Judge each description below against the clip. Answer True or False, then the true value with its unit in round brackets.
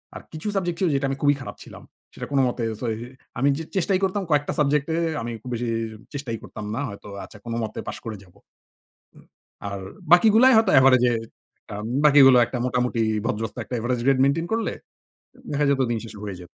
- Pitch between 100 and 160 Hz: True (135 Hz)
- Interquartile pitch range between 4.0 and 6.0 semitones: True (4.7 semitones)